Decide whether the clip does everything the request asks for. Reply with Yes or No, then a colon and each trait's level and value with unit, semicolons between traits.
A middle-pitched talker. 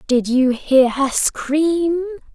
No: very high, 290 Hz